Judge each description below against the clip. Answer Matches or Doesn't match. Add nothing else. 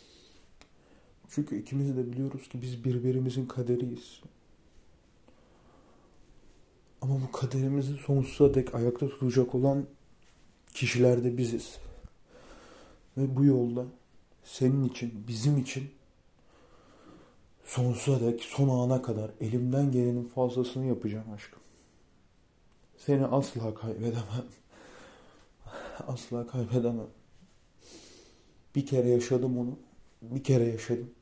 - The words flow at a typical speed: Doesn't match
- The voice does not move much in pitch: Matches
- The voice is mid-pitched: Doesn't match